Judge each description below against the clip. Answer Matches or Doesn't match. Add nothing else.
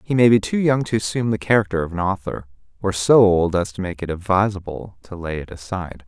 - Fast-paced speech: Matches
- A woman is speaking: Doesn't match